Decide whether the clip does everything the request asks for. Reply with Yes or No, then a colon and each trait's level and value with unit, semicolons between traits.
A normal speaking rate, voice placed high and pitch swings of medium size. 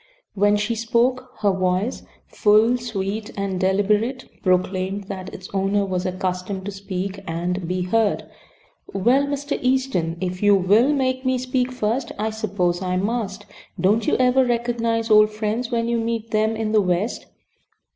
Yes: average, 155 wpm; high, 210 Hz; average, 3.7 semitones